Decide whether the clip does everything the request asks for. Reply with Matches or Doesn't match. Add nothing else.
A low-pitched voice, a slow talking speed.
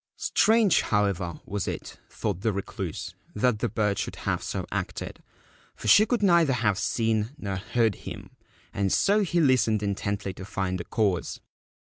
Doesn't match